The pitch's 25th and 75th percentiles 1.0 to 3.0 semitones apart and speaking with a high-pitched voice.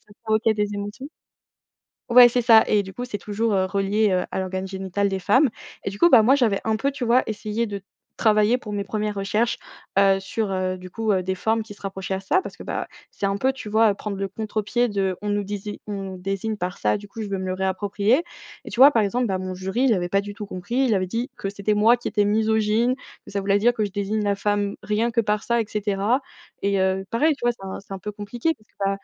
Yes: narrow, 2.5 semitones; high, 205 Hz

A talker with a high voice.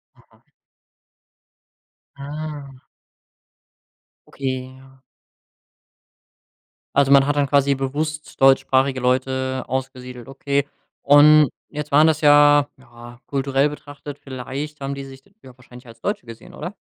No: low, 135 Hz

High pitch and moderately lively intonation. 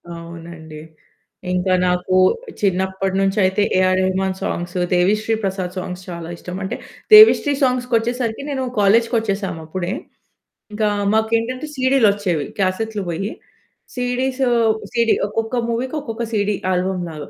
Yes: high, 195 Hz; average, 4.1 semitones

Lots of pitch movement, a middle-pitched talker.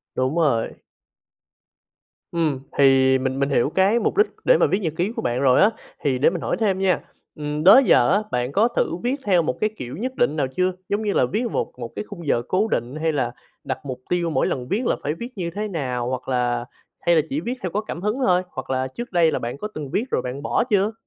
Yes: wide, 7.4 semitones; medium, 160 Hz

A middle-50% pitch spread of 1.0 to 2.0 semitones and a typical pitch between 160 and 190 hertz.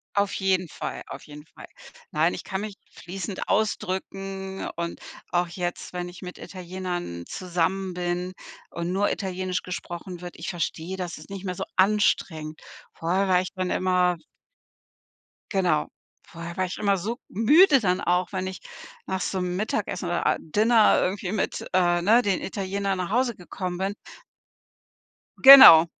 Yes: narrow, 1.7 semitones; medium, 185 Hz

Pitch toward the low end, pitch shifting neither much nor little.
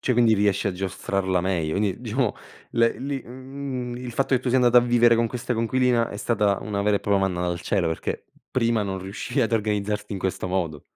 Yes: low, 110 Hz; average, 3.9 semitones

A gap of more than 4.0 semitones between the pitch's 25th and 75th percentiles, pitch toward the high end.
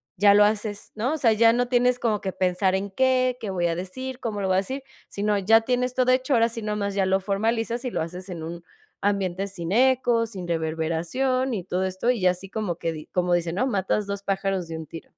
Yes: average, 4.4 semitones; high, 200 Hz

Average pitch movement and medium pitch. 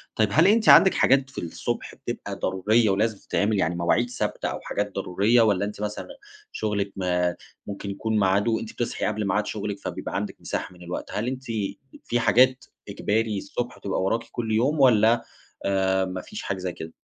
No: average, 3.3 semitones; low, 105 Hz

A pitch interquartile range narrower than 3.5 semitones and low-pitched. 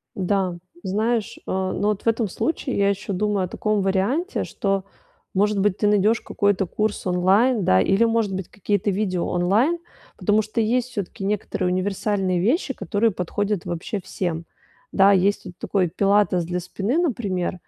No: narrow, 2.4 semitones; high, 200 Hz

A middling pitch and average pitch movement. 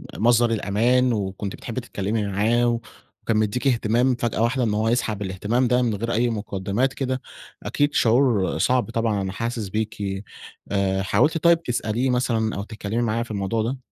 No: low, 115 Hz; average, 3.1 semitones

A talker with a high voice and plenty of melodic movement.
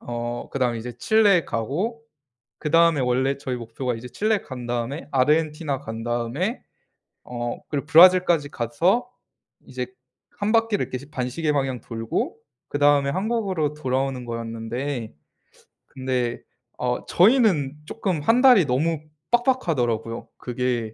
No: medium, 140 Hz; wide, 6.0 semitones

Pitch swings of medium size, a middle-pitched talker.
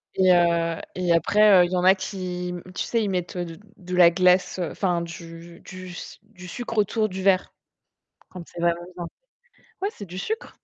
No: narrow, 1.8 semitones; medium, 180 Hz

